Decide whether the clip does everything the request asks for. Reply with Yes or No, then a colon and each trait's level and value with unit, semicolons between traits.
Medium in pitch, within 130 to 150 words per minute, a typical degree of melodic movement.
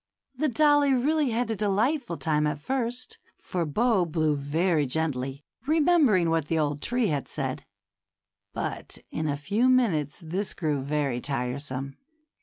No: medium, 165 Hz; average, 145 wpm; wide, 8.9 semitones